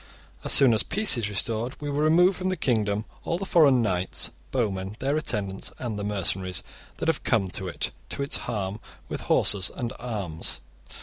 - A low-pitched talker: Yes, low, 110 Hz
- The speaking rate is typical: Yes, average, 190 wpm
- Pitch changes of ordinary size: No, wide, 6.2 semitones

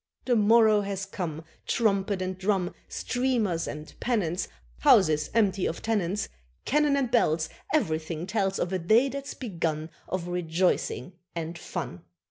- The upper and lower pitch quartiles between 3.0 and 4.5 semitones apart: No, average, 4.9 semitones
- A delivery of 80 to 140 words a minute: Yes, slow, 135 wpm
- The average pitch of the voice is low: No, high, 190 Hz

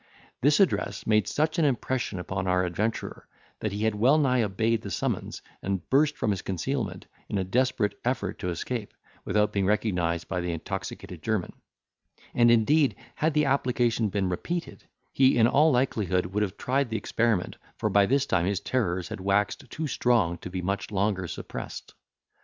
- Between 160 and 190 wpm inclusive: Yes, average, 175 wpm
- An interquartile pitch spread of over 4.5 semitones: Yes, average, 5.2 semitones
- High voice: No, low, 105 Hz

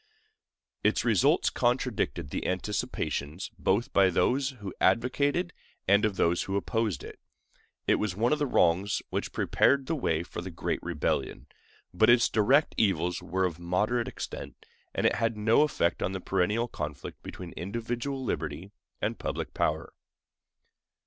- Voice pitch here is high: No, low, 100 Hz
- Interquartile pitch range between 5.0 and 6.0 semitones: Yes, average, 5.3 semitones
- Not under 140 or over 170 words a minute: Yes, average, 150 wpm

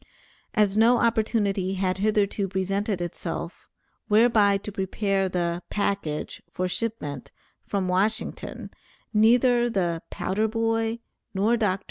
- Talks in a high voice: Yes, high, 200 Hz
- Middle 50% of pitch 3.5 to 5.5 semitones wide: No, average, 2.9 semitones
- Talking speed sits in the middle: No, slow, 115 wpm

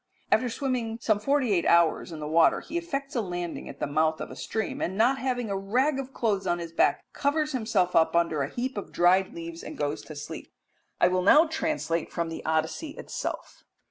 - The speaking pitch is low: No, high, 195 Hz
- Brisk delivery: Yes, fast, 215 wpm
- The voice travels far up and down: Yes, wide, 7.6 semitones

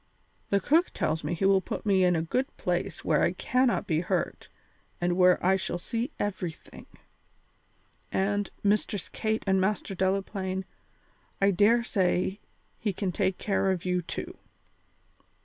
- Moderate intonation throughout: No, narrow, 2.2 semitones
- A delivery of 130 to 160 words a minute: Yes, average, 150 wpm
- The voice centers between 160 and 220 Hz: Yes, high, 190 Hz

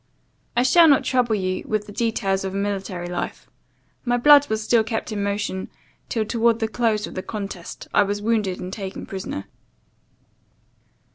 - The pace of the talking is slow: No, average, 170 wpm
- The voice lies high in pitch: Yes, high, 210 Hz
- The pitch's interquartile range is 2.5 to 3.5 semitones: Yes, average, 3.1 semitones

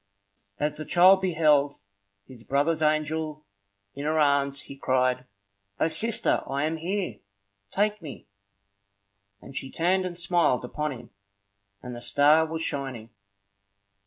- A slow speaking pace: Yes, slow, 130 wpm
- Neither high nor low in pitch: Yes, medium, 150 Hz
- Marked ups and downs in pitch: No, average, 3.2 semitones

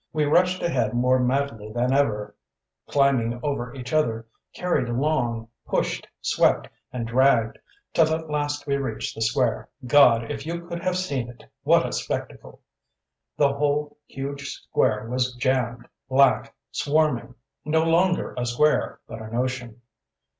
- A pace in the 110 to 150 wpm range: Yes, average, 145 wpm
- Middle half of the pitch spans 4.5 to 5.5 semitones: No, average, 3.8 semitones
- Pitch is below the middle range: Yes, low, 130 Hz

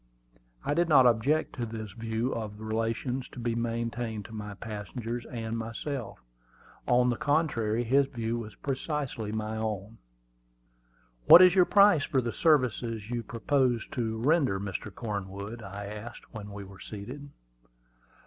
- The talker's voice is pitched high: No, low, 115 Hz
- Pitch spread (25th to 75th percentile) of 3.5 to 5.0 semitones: No, average, 3.1 semitones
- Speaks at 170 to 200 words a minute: No, average, 150 wpm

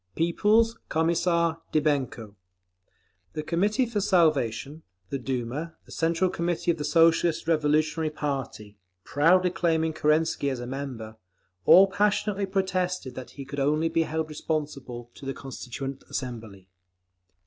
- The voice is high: No, medium, 155 Hz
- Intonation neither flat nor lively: Yes, average, 4.4 semitones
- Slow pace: Yes, slow, 125 wpm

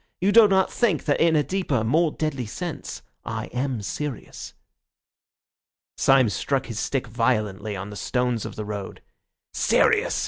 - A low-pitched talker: Yes, low, 125 Hz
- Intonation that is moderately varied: No, wide, 6.3 semitones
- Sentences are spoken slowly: No, average, 160 wpm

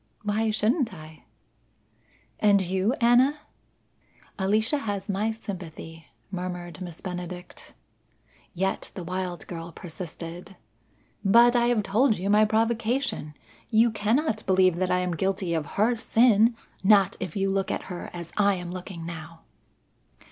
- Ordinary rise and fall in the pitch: Yes, average, 3.8 semitones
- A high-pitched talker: Yes, high, 195 Hz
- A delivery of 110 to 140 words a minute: Yes, slow, 135 wpm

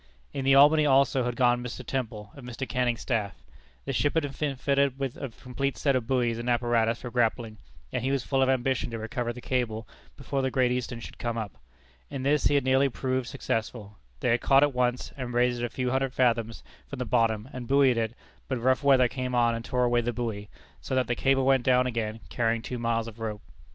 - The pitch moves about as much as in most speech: No, narrow, 2.3 semitones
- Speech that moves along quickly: Yes, fast, 230 wpm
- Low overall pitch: Yes, low, 125 Hz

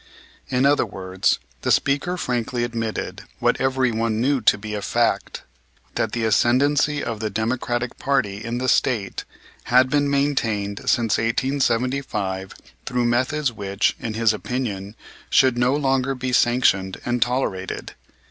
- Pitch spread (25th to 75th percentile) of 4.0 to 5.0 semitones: No, average, 3.4 semitones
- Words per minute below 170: Yes, average, 140 wpm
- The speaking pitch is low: Yes, low, 120 Hz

